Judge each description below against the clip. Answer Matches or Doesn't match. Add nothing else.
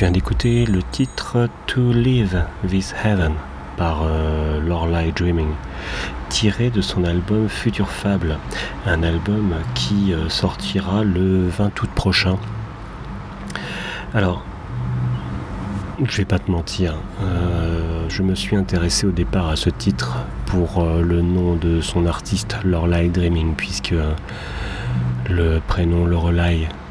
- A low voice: Matches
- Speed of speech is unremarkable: Doesn't match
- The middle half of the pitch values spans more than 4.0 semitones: Doesn't match